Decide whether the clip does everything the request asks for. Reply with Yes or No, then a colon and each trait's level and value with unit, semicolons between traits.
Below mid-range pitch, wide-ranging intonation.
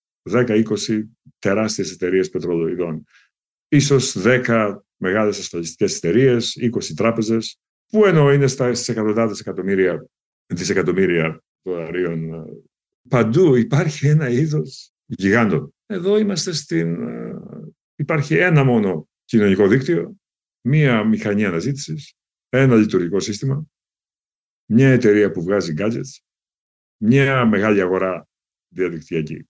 Yes: low, 115 Hz; wide, 5.7 semitones